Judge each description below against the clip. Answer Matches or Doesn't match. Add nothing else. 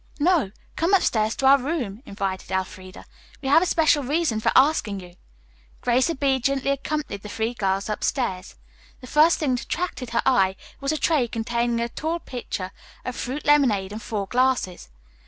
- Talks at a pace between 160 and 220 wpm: Matches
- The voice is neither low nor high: Doesn't match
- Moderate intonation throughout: Doesn't match